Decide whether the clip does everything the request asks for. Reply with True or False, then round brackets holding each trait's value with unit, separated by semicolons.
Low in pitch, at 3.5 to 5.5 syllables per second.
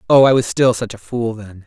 True (115 Hz; 5.4 syllables/s)